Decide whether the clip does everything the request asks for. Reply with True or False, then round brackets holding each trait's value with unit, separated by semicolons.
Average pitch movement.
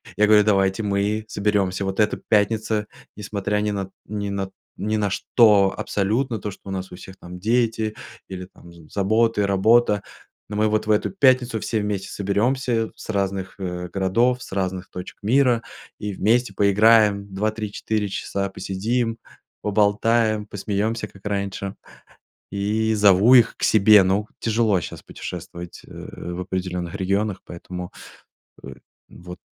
False (2.2 semitones)